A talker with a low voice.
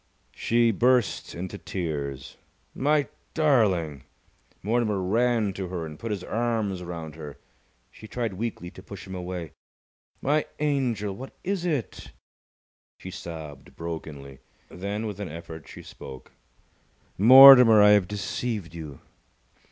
Yes: low, 100 Hz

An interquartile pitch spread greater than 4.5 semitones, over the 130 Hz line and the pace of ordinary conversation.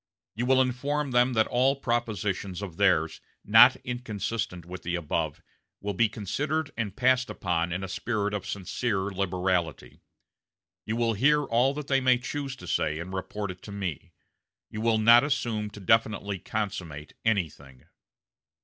No: average, 4.9 semitones; low, 105 Hz; average, 155 wpm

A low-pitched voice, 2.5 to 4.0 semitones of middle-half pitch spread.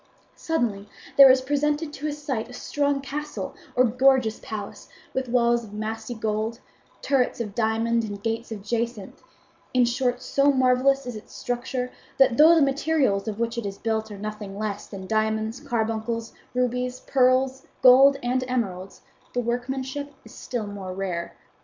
No: high, 240 Hz; average, 3.4 semitones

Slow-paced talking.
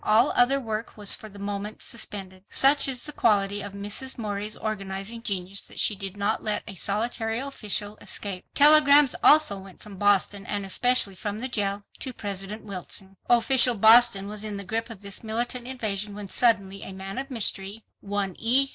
No: average, 180 wpm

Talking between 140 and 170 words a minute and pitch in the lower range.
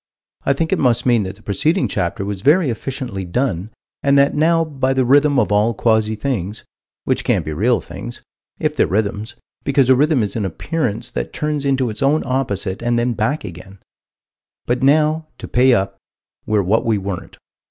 No: average, 190 wpm; low, 120 Hz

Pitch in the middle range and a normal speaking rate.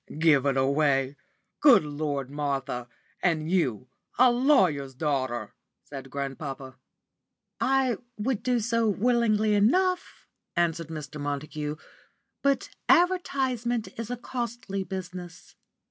No: medium, 175 Hz; slow, 105 wpm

